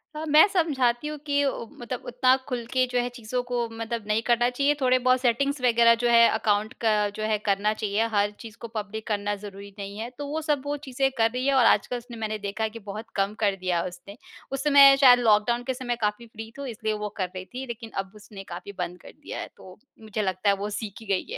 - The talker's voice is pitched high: Yes, high, 230 Hz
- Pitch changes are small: No, average, 3.5 semitones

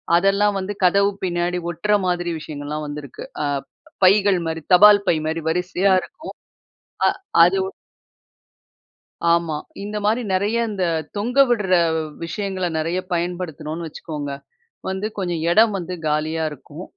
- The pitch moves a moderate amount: Yes, average, 3.5 semitones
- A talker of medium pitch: Yes, medium, 180 Hz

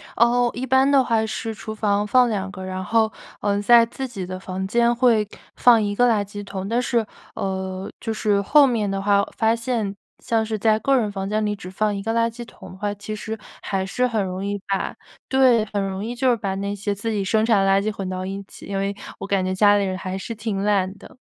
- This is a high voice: Yes, high, 210 Hz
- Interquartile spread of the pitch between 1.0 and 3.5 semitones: Yes, average, 2.8 semitones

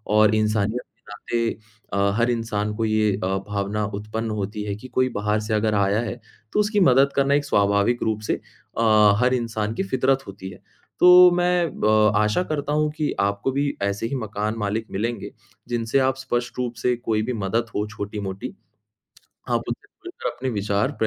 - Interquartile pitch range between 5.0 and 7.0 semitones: No, average, 3.5 semitones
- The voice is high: No, low, 110 Hz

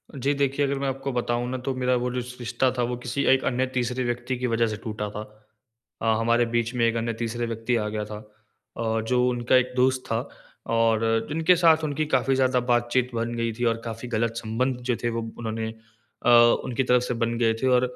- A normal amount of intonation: No, narrow, 1.9 semitones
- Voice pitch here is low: Yes, low, 120 Hz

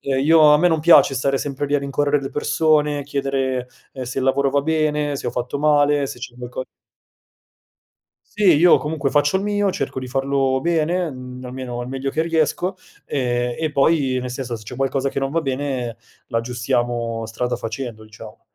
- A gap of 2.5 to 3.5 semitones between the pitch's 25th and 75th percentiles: Yes, average, 2.9 semitones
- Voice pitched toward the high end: No, low, 135 Hz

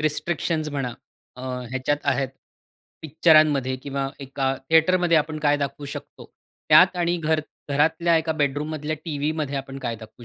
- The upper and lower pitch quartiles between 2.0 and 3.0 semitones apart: Yes, narrow, 2.6 semitones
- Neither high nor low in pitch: Yes, medium, 150 Hz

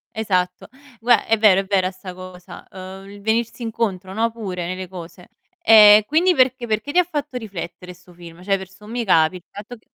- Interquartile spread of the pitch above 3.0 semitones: Yes, average, 3.7 semitones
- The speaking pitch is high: Yes, high, 200 Hz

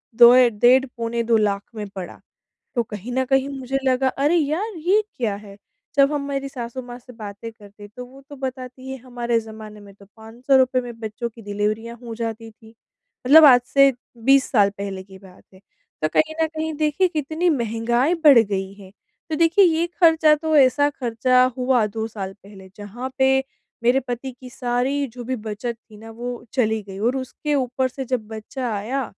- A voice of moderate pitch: No, high, 245 Hz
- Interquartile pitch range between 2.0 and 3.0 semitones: No, average, 3.6 semitones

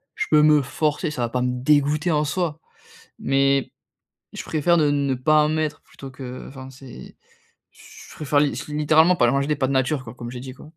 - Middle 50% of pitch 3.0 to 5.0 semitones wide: No, narrow, 2.6 semitones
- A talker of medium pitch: Yes, medium, 145 Hz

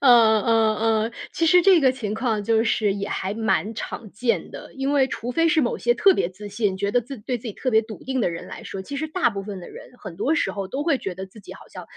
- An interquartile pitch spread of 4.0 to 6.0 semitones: Yes, average, 4.5 semitones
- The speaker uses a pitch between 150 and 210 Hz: No, high, 225 Hz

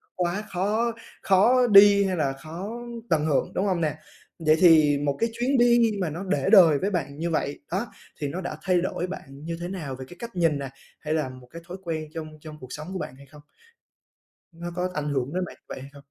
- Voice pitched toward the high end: No, medium, 170 Hz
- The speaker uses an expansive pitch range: No, average, 4.3 semitones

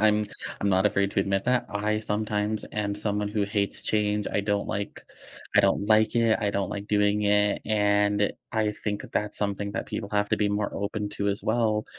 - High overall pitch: No, low, 105 Hz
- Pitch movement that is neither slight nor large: No, narrow, 0.8 semitones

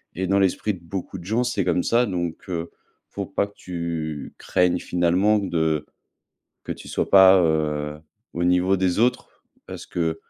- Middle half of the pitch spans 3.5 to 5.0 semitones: No, average, 2.8 semitones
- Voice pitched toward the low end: Yes, very low, 90 Hz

